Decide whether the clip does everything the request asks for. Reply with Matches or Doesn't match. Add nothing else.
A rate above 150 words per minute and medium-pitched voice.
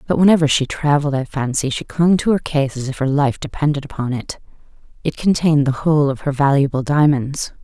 Matches